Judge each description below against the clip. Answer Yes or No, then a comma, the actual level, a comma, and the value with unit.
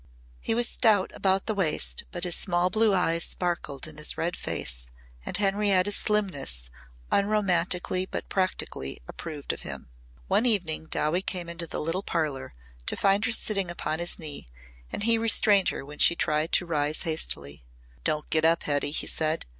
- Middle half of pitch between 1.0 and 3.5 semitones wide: No, average, 4.3 semitones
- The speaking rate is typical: Yes, average, 170 wpm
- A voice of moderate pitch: Yes, medium, 175 Hz